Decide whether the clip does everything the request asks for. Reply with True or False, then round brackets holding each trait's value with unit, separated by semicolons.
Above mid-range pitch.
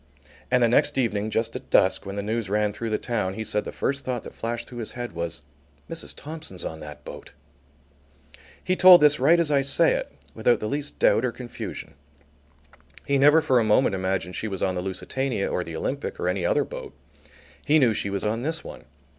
False (115 Hz)